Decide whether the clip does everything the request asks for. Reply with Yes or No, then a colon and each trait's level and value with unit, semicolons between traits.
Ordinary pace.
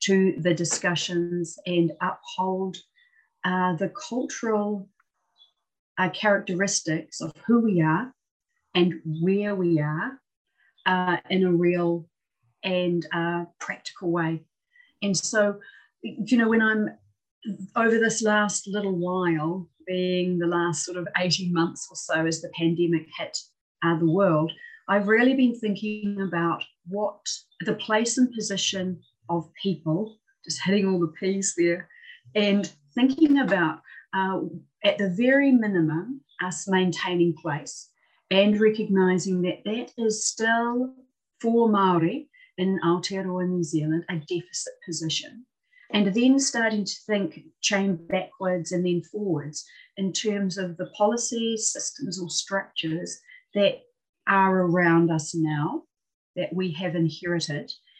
No: slow, 130 wpm